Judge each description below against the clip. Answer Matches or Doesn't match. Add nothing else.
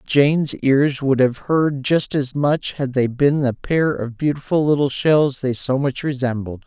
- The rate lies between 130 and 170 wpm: Doesn't match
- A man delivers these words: Matches